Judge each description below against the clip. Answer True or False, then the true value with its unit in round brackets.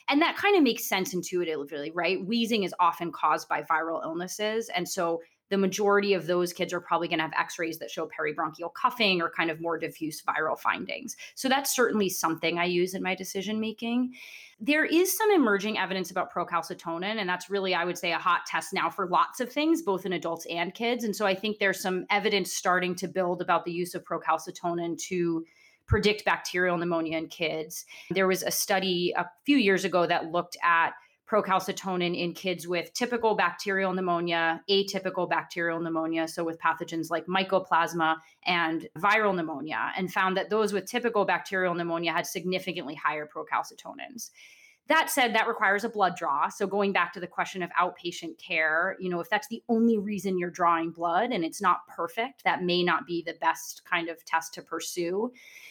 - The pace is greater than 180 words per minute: True (195 wpm)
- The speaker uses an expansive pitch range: False (3.2 semitones)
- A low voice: False (180 Hz)